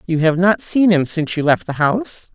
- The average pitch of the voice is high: No, medium, 175 Hz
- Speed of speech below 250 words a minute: No, fast, 255 wpm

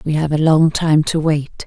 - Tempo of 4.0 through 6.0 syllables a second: Yes, 4.5 syllables/s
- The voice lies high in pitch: No, medium, 155 Hz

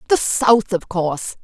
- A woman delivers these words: Yes, female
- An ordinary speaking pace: Yes, average, 165 wpm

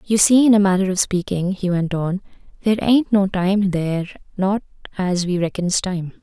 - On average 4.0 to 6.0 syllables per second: Yes, 5.0 syllables/s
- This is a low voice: No, high, 190 Hz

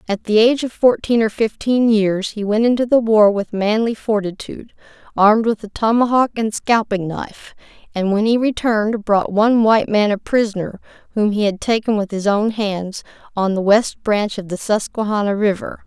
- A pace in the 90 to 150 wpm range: No, average, 185 wpm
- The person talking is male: No, female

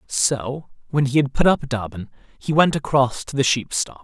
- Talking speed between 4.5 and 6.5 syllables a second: Yes, 4.6 syllables/s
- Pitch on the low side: Yes, low, 130 Hz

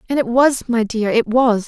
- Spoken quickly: Yes, fast, 250 wpm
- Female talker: Yes, female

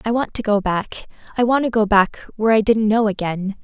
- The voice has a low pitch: No, high, 215 Hz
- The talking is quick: Yes, fast, 215 wpm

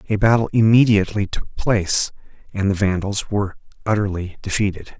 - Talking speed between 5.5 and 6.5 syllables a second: Yes, 5.8 syllables/s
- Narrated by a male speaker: Yes, male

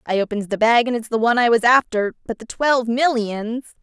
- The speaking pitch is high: Yes, high, 230 Hz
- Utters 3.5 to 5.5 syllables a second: No, 5.8 syllables/s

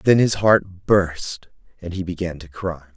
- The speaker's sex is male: Yes, male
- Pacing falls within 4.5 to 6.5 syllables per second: No, 4.0 syllables/s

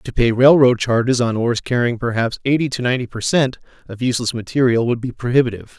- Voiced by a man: Yes, male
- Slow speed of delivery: No, average, 195 wpm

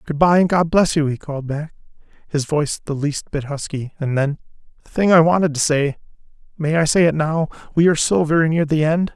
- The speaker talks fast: Yes, fast, 210 wpm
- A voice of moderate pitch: Yes, medium, 155 Hz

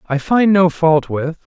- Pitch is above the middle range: No, medium, 165 Hz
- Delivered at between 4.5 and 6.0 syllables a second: No, 3.9 syllables/s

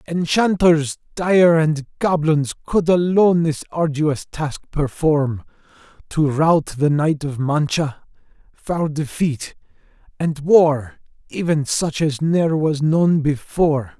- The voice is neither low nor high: Yes, medium, 155 Hz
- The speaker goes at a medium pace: No, slow, 115 wpm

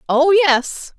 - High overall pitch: Yes, very high, 320 Hz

